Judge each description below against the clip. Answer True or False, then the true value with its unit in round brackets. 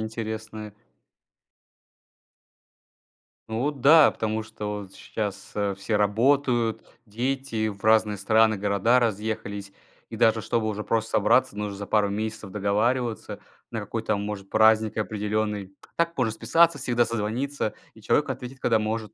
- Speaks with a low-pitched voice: True (110 Hz)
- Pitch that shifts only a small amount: True (1.9 semitones)